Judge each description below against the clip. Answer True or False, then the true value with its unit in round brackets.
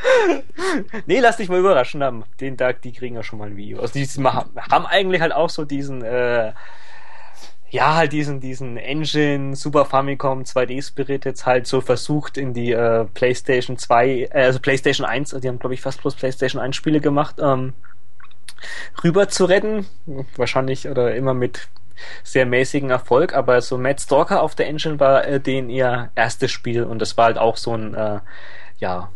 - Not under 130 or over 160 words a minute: False (175 wpm)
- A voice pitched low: True (130 Hz)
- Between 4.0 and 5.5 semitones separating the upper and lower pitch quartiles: False (2.5 semitones)